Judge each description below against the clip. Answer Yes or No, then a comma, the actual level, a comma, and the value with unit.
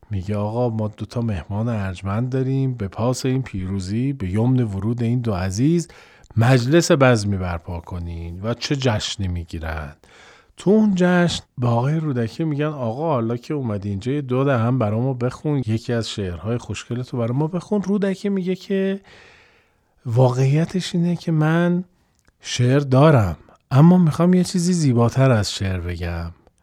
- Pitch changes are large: Yes, wide, 7.1 semitones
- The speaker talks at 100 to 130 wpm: No, average, 150 wpm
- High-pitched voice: No, low, 125 Hz